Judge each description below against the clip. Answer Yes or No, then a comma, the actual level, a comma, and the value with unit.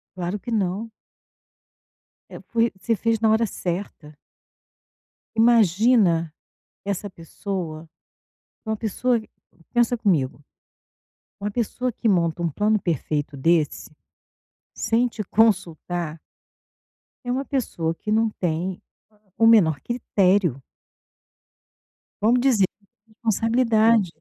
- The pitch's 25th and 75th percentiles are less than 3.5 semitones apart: No, average, 4.9 semitones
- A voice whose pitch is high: Yes, high, 205 Hz